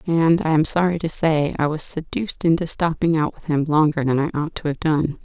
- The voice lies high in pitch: No, medium, 155 Hz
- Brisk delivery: Yes, fast, 240 wpm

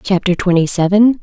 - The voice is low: No, high, 190 Hz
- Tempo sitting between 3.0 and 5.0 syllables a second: No, 5.3 syllables/s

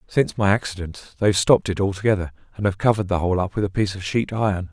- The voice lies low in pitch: Yes, very low, 95 Hz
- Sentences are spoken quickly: Yes, fast, 255 wpm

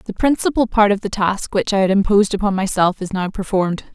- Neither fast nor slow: No, fast, 230 wpm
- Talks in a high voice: Yes, high, 200 Hz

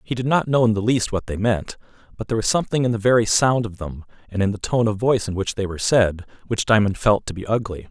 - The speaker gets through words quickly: Yes, fast, 280 wpm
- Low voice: Yes, low, 110 Hz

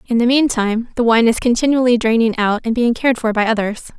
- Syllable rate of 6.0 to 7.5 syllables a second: Yes, 6.2 syllables/s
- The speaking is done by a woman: Yes, female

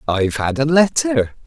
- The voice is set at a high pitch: No, medium, 140 Hz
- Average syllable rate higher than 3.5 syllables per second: Yes, 5.0 syllables/s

